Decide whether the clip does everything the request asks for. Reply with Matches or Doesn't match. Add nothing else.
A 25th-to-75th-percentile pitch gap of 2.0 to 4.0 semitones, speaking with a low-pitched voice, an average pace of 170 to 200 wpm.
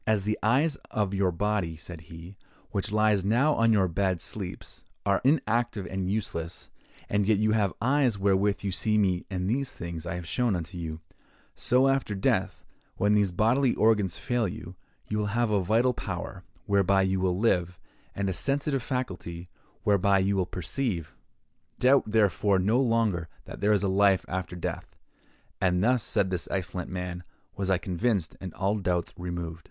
Matches